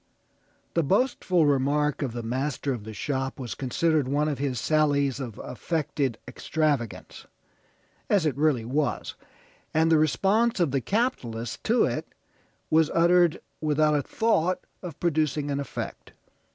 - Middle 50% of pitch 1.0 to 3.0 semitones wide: No, average, 3.5 semitones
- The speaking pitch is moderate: Yes, medium, 150 Hz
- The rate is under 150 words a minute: Yes, average, 140 wpm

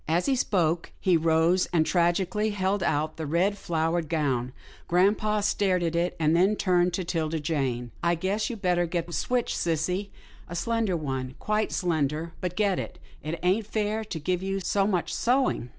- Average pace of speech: Yes, average, 195 wpm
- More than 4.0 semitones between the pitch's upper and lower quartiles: No, average, 3.6 semitones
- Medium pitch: Yes, medium, 175 Hz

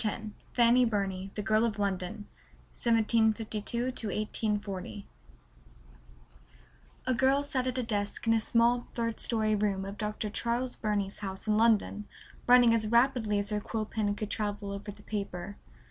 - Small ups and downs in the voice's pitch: Yes, narrow, 2.3 semitones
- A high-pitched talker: Yes, high, 215 Hz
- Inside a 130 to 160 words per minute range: Yes, average, 150 wpm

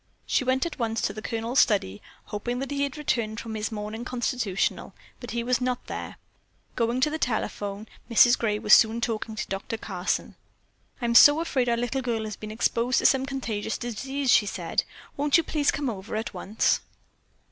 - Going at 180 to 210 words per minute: Yes, average, 190 wpm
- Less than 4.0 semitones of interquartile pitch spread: Yes, average, 3.1 semitones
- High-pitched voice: Yes, high, 235 Hz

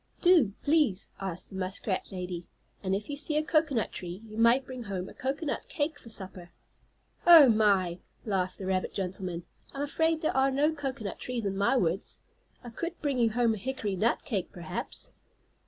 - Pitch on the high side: Yes, high, 225 Hz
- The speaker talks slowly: No, average, 185 wpm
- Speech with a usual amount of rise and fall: No, wide, 6.9 semitones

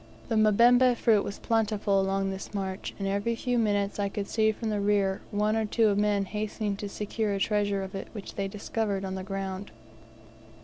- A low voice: No, high, 205 Hz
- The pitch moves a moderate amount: No, narrow, 1.7 semitones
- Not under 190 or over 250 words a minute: Yes, average, 195 wpm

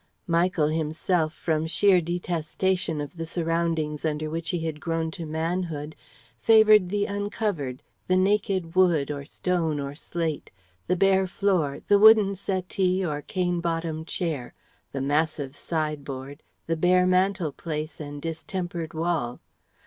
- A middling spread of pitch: Yes, average, 3.1 semitones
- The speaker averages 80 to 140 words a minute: Yes, slow, 135 wpm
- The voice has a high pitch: No, medium, 165 Hz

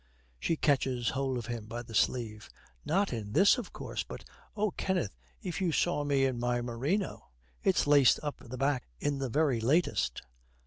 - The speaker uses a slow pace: No, average, 180 wpm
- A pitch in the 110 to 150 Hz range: Yes, low, 135 Hz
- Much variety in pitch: No, average, 5.0 semitones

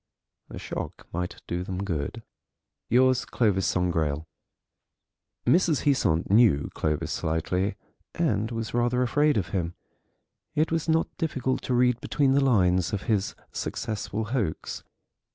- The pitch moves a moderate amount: No, wide, 6.3 semitones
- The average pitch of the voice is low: Yes, low, 110 Hz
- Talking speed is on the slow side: Yes, slow, 130 wpm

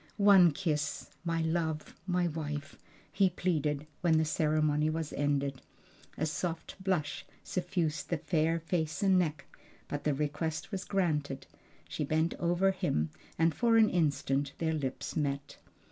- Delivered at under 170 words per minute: Yes, average, 145 wpm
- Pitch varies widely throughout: No, average, 2.9 semitones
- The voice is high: No, medium, 160 Hz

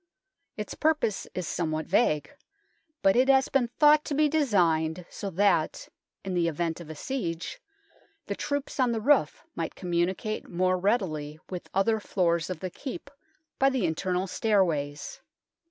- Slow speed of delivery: No, average, 150 wpm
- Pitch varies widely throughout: Yes, wide, 6.8 semitones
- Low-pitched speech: No, high, 190 Hz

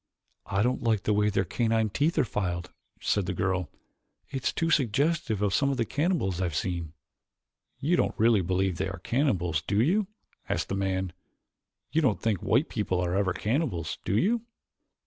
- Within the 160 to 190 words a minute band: Yes, average, 185 wpm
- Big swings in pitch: Yes, wide, 6.3 semitones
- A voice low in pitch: Yes, low, 105 Hz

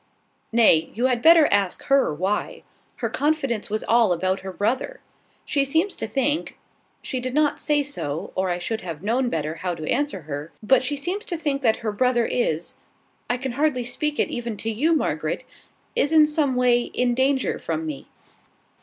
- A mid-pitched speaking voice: No, high, 245 Hz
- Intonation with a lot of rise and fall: Yes, wide, 6.4 semitones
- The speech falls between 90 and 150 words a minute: No, average, 190 wpm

